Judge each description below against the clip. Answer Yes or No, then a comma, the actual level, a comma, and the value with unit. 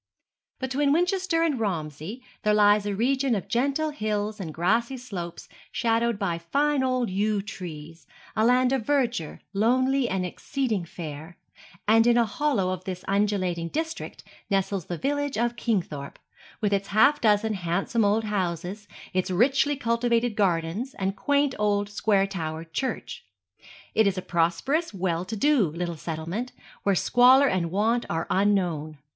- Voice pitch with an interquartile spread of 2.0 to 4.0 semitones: No, wide, 5.6 semitones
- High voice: Yes, high, 210 Hz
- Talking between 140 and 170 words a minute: Yes, average, 150 wpm